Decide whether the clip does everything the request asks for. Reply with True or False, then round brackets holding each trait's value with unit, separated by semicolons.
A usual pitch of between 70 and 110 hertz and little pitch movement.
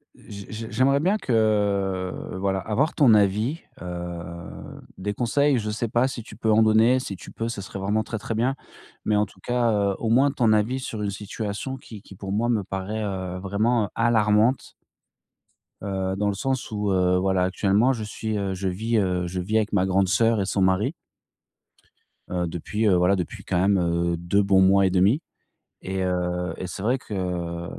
False (100 Hz; 3.1 semitones)